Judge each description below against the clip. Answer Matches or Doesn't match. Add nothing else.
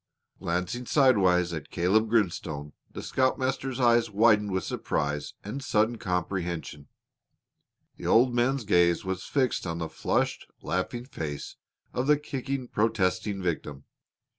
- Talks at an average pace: Doesn't match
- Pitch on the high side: Doesn't match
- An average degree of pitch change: Doesn't match